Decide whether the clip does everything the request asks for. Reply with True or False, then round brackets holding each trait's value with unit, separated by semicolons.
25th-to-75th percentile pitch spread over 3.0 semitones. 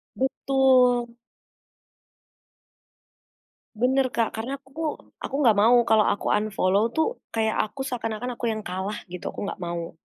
True (3.5 semitones)